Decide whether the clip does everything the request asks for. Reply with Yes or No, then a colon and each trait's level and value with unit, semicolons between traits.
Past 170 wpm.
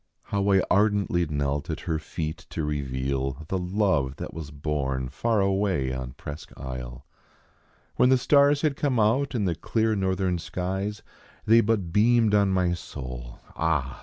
No: average, 160 wpm